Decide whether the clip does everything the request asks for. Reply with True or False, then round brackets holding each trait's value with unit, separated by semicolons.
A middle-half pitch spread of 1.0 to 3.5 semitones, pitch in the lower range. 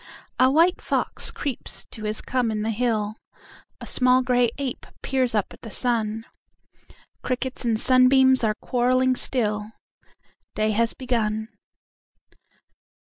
False (2.8 semitones; 245 Hz)